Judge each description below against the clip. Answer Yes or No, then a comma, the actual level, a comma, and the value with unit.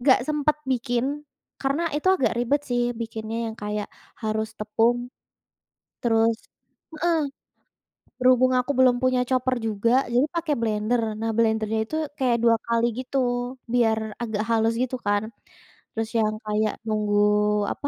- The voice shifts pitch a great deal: No, average, 2.7 semitones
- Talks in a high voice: Yes, high, 230 Hz